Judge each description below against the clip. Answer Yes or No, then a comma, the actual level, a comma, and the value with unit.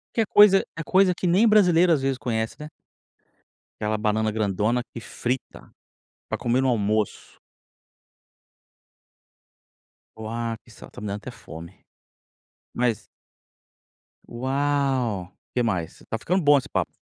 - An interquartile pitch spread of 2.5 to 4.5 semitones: No, average, 5.2 semitones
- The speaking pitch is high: No, low, 120 Hz